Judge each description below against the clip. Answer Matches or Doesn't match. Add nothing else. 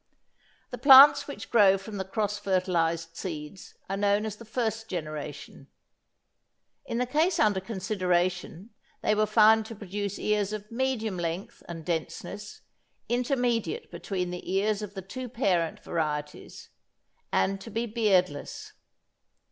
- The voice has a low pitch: Doesn't match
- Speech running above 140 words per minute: Doesn't match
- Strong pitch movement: Doesn't match